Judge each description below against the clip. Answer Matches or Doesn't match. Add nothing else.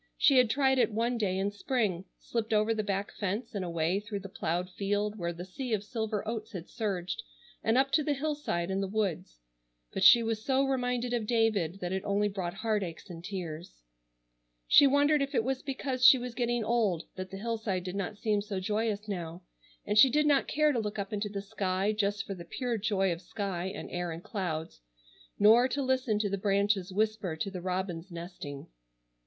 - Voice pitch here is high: Matches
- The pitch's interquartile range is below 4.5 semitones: Matches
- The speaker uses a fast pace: Matches